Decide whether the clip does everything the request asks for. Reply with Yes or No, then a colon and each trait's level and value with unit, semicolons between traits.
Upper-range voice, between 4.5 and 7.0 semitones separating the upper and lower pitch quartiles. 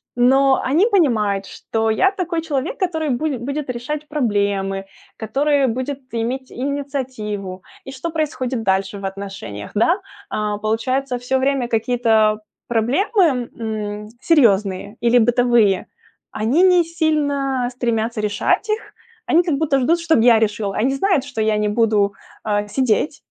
Yes: high, 245 Hz; average, 5.0 semitones